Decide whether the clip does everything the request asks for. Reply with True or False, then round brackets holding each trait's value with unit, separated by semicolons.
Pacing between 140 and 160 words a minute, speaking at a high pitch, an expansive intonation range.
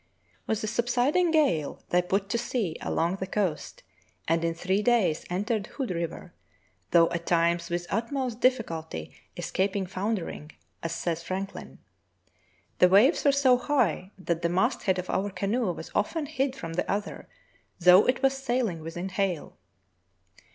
True (155 wpm; 195 Hz; 5.9 semitones)